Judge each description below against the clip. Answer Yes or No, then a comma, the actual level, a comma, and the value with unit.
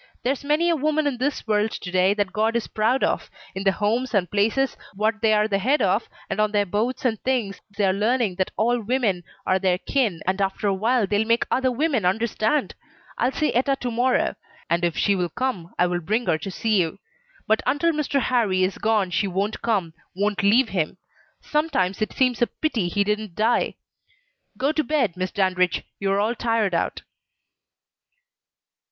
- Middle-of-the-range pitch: No, high, 215 Hz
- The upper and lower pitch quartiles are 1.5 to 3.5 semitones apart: No, average, 4.5 semitones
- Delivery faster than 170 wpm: Yes, average, 195 wpm